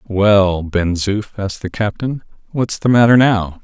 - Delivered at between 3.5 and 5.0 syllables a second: Yes, 4.2 syllables/s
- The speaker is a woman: No, male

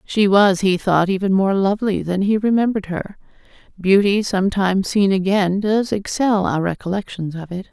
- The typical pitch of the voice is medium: No, high, 195 Hz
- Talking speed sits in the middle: Yes, average, 165 wpm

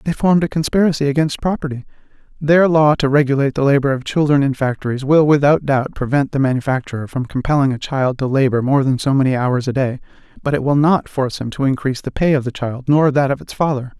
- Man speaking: Yes, male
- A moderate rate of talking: No, fast, 225 wpm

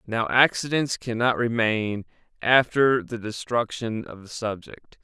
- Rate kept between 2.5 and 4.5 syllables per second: Yes, 4.0 syllables/s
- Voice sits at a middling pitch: No, low, 115 Hz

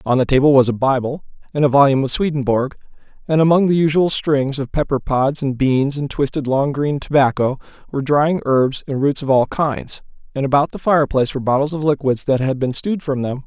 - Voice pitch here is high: No, medium, 140 Hz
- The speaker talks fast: Yes, fast, 215 wpm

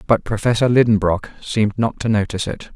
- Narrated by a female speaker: No, male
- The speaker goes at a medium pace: Yes, average, 175 wpm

